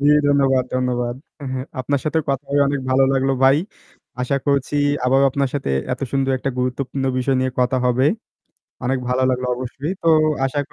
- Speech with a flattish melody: Yes, narrow, 1.6 semitones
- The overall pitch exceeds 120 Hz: Yes, low, 135 Hz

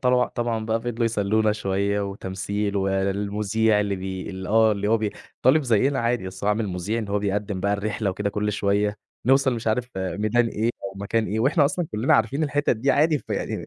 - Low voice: Yes, low, 105 Hz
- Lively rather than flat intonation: No, narrow, 2.6 semitones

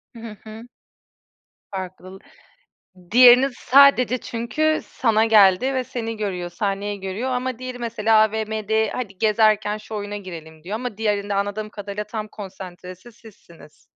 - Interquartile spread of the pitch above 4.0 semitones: No, average, 2.8 semitones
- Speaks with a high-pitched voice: Yes, high, 215 Hz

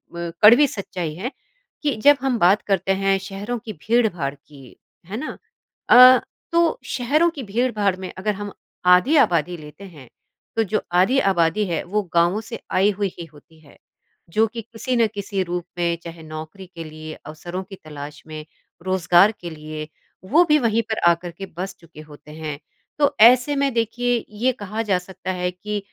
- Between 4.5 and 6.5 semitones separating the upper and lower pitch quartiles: Yes, average, 5.2 semitones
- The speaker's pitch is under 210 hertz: Yes, high, 190 Hz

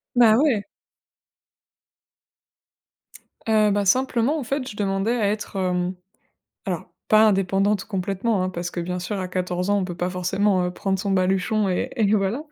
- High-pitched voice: Yes, high, 195 Hz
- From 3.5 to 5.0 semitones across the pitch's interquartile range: No, average, 2.8 semitones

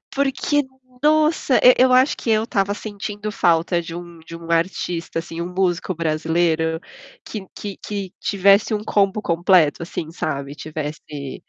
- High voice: No, medium, 180 Hz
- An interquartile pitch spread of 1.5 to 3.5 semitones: No, average, 4.2 semitones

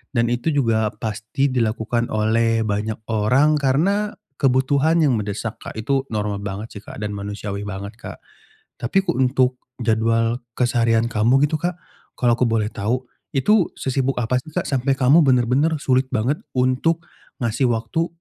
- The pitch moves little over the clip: No, average, 3.6 semitones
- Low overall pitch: Yes, low, 120 Hz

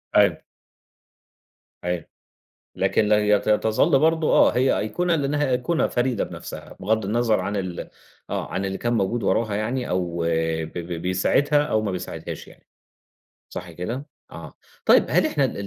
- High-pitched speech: No, low, 105 Hz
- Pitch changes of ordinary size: No, wide, 5.9 semitones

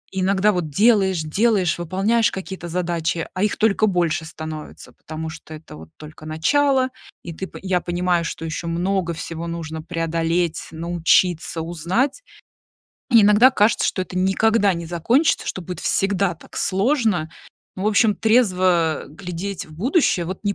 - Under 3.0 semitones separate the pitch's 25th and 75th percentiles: No, average, 3.6 semitones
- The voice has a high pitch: No, medium, 180 Hz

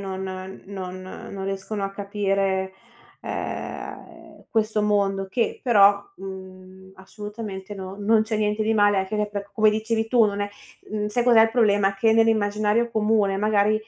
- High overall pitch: Yes, high, 205 Hz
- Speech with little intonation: Yes, narrow, 1.9 semitones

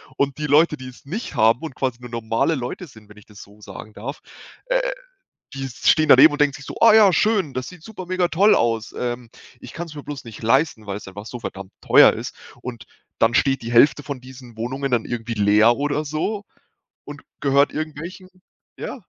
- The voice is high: No, low, 135 Hz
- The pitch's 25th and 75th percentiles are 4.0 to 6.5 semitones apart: Yes, average, 5.1 semitones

